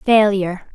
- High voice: Yes, high, 200 Hz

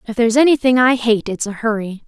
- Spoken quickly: Yes, fast, 230 wpm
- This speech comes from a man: No, female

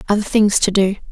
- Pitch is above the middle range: Yes, high, 205 Hz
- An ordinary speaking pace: No, fast, 215 wpm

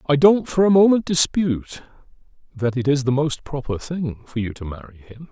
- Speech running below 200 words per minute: No, fast, 205 wpm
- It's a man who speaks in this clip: Yes, male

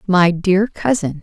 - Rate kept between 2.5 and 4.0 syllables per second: Yes, 3.7 syllables/s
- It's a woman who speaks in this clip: Yes, female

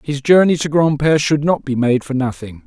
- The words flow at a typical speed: No, fast, 225 wpm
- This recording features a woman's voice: No, male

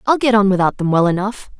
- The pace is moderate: No, fast, 265 wpm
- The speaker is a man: No, female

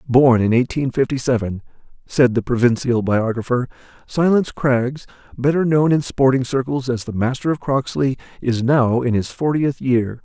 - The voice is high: No, low, 125 Hz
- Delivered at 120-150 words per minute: No, average, 160 wpm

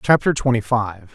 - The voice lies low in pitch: Yes, low, 120 Hz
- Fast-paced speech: No, average, 155 wpm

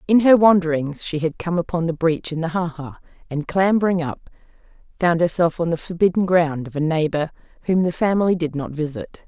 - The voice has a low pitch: No, medium, 170 Hz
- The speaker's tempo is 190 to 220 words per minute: Yes, average, 200 wpm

